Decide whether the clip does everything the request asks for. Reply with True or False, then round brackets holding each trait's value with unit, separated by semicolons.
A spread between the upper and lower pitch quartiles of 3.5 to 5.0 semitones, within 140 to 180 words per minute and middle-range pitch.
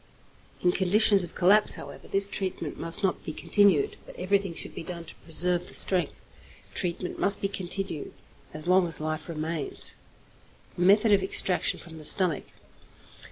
False (2.9 semitones; 160 wpm; 180 Hz)